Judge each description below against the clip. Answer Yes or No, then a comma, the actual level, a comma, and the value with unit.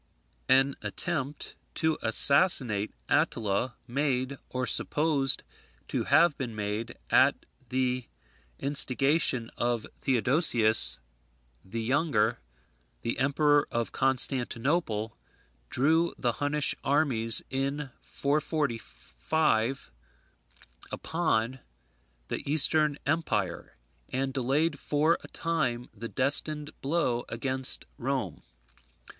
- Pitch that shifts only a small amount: No, average, 4.1 semitones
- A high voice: No, low, 135 Hz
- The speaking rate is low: Yes, slow, 90 wpm